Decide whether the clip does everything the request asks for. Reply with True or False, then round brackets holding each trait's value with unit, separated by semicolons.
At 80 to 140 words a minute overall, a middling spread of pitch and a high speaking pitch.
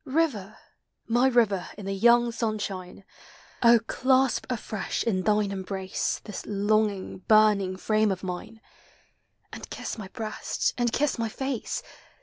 True (135 wpm; 3.2 semitones; 215 Hz)